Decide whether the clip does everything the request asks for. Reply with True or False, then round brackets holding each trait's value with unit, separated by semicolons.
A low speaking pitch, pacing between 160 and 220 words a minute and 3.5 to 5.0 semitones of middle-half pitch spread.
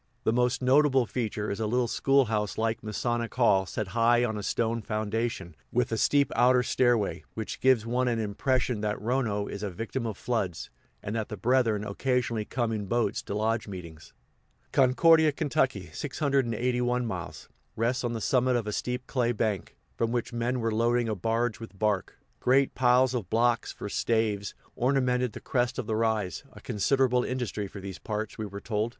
False (115 Hz; 185 wpm; 2.8 semitones)